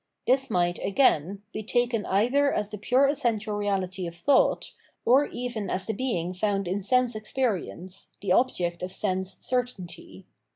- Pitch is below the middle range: No, high, 205 Hz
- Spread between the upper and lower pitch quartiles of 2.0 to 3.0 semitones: No, average, 5.0 semitones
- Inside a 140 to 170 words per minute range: Yes, average, 155 wpm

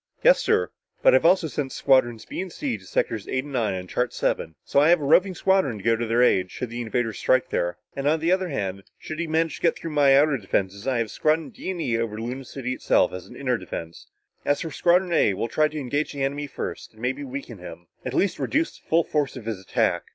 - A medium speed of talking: No, fast, 255 wpm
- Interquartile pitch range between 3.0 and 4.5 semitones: No, wide, 5.6 semitones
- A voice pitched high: No, low, 135 Hz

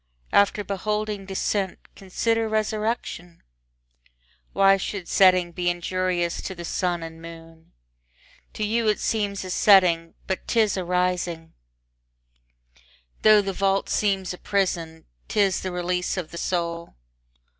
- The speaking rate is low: Yes, slow, 125 wpm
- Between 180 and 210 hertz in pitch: Yes, medium, 185 Hz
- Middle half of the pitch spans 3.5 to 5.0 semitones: No, average, 2.7 semitones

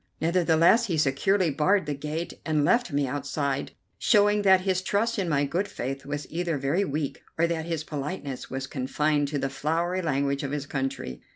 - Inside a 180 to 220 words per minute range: Yes, average, 185 wpm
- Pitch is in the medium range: Yes, medium, 150 Hz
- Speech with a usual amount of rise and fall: Yes, average, 4.2 semitones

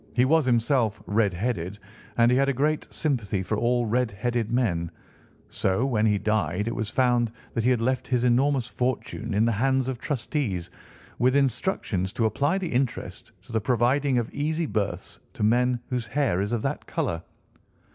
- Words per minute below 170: No, average, 185 wpm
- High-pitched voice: No, low, 120 Hz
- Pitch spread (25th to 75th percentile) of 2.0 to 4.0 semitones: Yes, average, 3.4 semitones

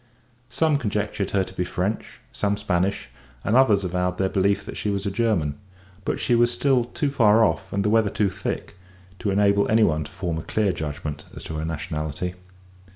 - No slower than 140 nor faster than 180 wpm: No, average, 200 wpm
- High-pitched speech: No, low, 100 Hz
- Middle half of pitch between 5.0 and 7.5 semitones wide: No, average, 3.4 semitones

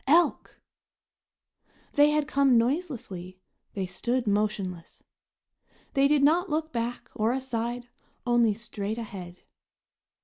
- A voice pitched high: Yes, high, 240 Hz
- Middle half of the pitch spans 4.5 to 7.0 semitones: Yes, average, 5.2 semitones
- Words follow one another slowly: Yes, slow, 105 wpm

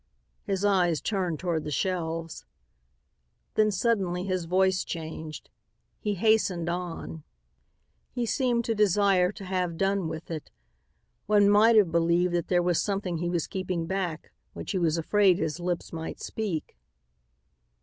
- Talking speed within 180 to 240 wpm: No, average, 145 wpm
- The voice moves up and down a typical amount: Yes, average, 3.1 semitones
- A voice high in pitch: No, medium, 180 Hz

